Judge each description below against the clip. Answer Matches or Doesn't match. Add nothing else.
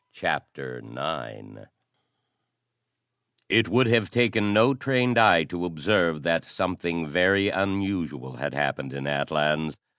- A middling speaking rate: Doesn't match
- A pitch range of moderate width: Doesn't match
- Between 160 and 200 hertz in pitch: Doesn't match